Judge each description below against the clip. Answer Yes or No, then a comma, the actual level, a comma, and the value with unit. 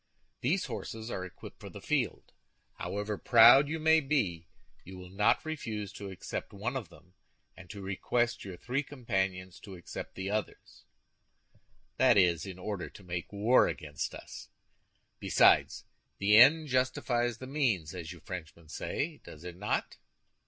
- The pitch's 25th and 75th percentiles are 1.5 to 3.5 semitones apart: No, wide, 5.4 semitones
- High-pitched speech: No, low, 105 Hz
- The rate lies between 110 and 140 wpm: No, average, 150 wpm